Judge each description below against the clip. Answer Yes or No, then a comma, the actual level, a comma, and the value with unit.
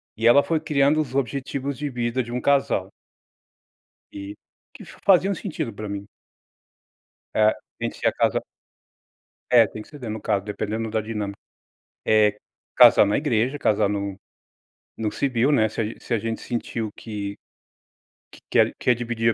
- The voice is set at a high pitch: No, low, 115 Hz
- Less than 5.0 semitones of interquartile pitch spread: Yes, average, 4.2 semitones